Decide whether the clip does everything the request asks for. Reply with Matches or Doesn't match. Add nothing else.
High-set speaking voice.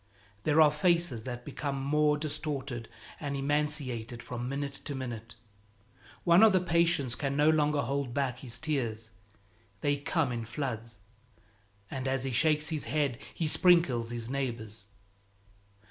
Doesn't match